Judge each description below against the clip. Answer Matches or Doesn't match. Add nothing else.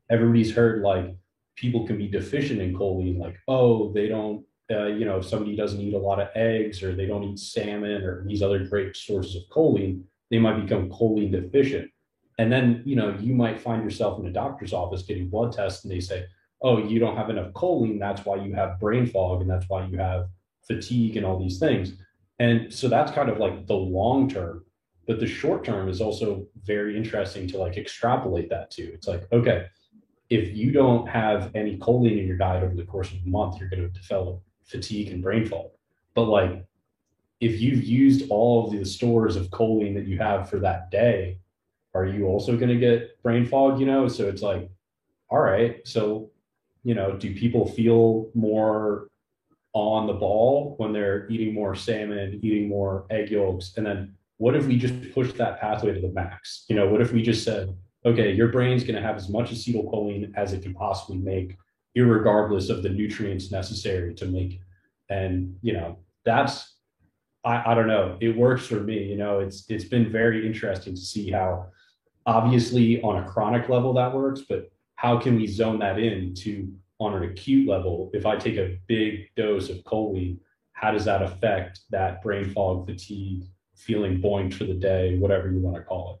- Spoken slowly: Doesn't match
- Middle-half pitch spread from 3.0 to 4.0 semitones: Matches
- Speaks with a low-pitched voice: Matches